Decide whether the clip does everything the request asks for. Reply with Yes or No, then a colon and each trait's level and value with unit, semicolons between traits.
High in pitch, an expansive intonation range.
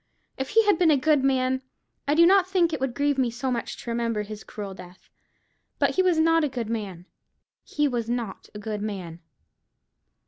Yes: very high, 255 Hz; wide, 6.2 semitones